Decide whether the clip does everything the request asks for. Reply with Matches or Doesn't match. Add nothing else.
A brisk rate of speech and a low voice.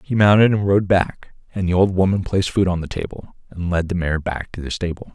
Matches